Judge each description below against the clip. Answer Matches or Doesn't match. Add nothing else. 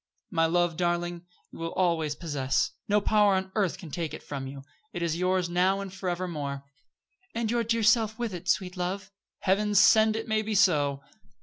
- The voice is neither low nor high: Matches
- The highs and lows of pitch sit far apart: Doesn't match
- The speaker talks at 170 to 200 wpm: Matches